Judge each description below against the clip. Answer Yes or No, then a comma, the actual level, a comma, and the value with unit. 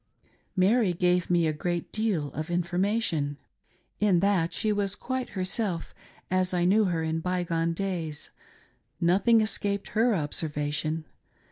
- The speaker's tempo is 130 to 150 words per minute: Yes, slow, 135 wpm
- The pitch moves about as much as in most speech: Yes, average, 3.6 semitones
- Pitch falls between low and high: Yes, medium, 180 Hz